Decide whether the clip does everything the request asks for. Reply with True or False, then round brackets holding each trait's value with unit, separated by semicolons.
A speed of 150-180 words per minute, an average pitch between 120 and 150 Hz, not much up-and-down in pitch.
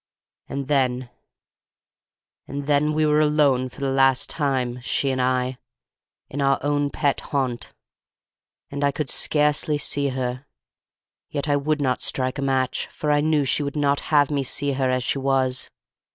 True (160 wpm; 140 Hz; 2.0 semitones)